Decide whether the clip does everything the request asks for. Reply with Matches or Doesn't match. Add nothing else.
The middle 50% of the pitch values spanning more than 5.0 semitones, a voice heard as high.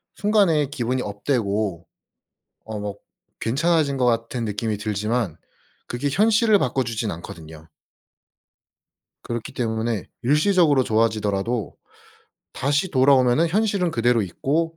Doesn't match